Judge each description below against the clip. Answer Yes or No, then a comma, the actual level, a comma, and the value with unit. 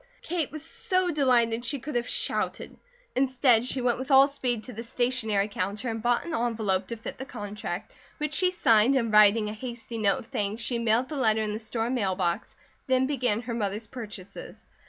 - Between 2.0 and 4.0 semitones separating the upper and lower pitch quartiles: Yes, average, 3.4 semitones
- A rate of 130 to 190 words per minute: No, average, 200 wpm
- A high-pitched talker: Yes, high, 235 Hz